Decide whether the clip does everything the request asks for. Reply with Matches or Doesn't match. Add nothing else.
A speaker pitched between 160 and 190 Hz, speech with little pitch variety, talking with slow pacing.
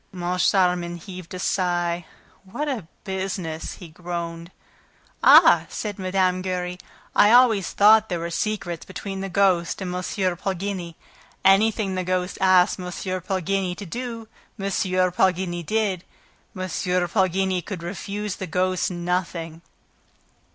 Matches